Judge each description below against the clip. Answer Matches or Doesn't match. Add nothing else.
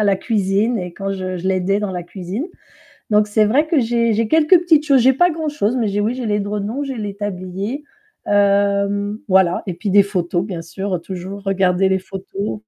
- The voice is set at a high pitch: Matches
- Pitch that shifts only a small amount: Doesn't match